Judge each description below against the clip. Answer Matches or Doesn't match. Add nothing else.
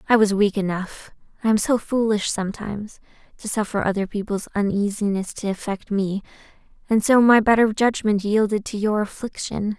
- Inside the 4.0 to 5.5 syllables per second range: Matches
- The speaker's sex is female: Matches